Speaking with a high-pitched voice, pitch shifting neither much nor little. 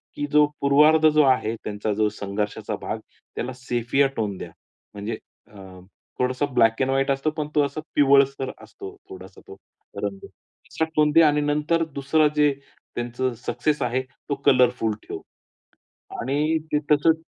No: medium, 140 Hz; average, 3.8 semitones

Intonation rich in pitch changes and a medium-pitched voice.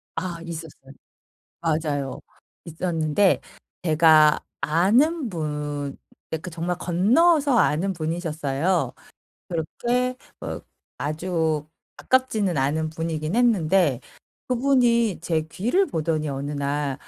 No: average, 4.6 semitones; medium, 165 Hz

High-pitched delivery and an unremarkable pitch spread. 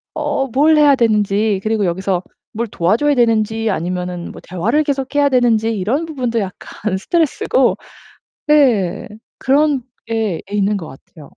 No: high, 225 Hz; wide, 5.8 semitones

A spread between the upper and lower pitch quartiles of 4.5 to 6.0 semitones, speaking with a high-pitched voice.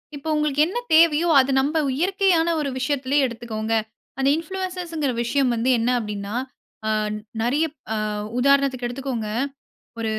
Yes: average, 5.1 semitones; very high, 275 Hz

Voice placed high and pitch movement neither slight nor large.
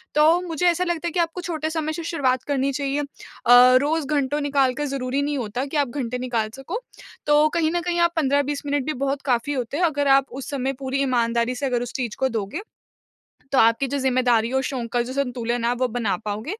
Yes: very high, 275 Hz; average, 3.2 semitones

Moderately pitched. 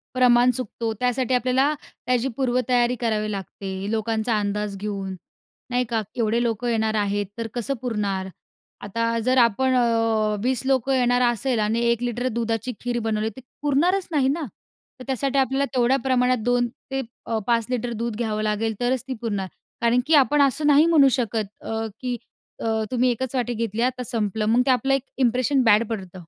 No: high, 240 Hz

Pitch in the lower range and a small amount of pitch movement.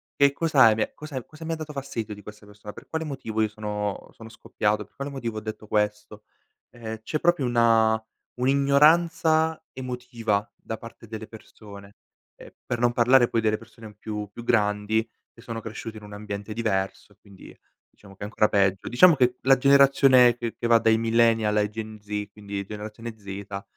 No: low, 110 Hz; average, 3.1 semitones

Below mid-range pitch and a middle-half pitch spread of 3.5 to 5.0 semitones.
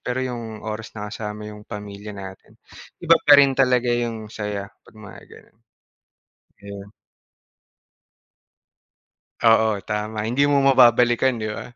No: low, 110 Hz; average, 2.9 semitones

